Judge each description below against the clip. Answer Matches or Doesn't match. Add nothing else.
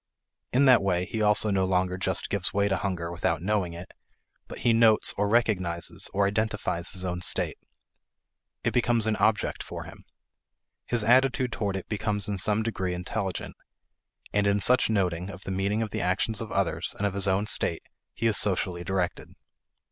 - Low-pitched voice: Matches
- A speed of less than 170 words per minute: Doesn't match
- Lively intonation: Doesn't match